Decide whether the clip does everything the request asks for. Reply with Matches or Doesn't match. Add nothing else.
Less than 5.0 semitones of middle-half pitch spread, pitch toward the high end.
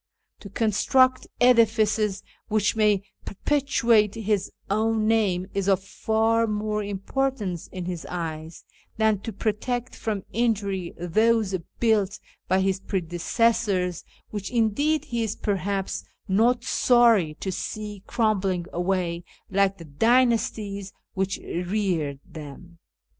Matches